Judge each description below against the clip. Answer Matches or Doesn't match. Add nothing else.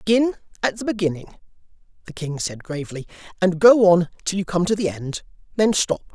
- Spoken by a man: Matches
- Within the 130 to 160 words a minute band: Doesn't match